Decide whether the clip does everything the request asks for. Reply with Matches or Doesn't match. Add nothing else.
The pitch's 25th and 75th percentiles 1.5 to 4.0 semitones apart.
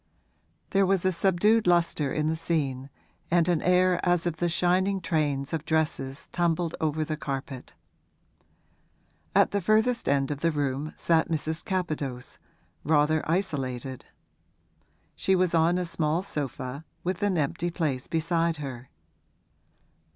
Matches